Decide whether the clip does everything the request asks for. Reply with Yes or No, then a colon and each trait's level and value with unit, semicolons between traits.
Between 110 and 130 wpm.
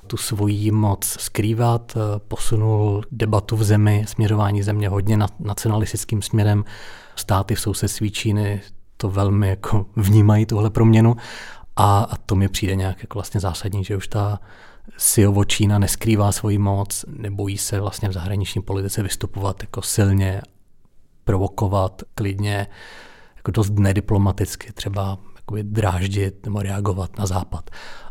Yes: average, 125 wpm